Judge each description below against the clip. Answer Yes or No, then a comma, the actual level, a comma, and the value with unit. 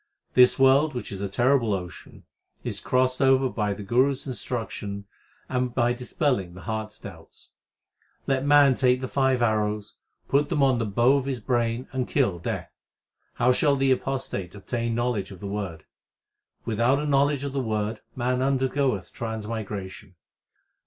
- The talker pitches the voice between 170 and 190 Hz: No, low, 120 Hz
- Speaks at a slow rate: No, average, 165 wpm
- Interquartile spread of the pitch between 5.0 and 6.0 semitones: No, average, 4.0 semitones